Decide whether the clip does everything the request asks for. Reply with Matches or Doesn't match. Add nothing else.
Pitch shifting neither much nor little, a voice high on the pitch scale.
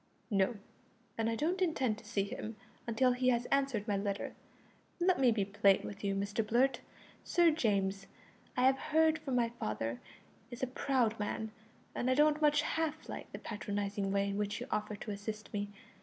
Matches